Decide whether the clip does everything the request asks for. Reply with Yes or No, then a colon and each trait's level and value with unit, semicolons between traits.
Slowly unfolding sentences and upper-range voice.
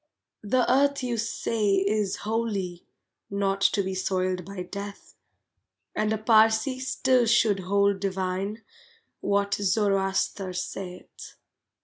Yes: slow, 110 wpm; high, 200 Hz